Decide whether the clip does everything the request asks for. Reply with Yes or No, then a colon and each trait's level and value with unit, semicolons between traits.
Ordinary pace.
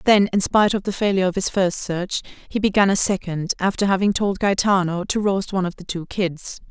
No: fast, 225 wpm